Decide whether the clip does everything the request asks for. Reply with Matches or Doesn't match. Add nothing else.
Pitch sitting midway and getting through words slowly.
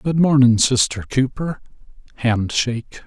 Doesn't match